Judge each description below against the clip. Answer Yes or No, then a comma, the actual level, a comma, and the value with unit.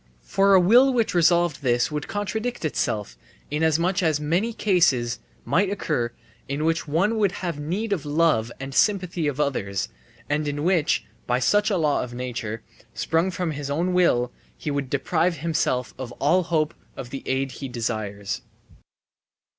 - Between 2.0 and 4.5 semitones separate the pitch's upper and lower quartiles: No, wide, 5.5 semitones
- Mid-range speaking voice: Yes, medium, 155 Hz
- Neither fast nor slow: Yes, average, 165 wpm